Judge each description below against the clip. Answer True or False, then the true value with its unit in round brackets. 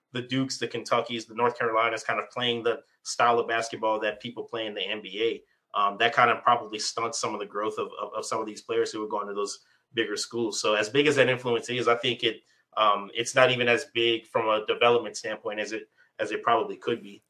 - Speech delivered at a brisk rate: True (245 wpm)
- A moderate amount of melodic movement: False (1.9 semitones)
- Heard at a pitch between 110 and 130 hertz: True (120 Hz)